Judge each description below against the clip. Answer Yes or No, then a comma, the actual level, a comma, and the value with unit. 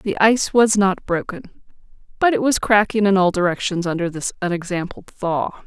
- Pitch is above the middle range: Yes, high, 195 Hz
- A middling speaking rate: Yes, average, 170 wpm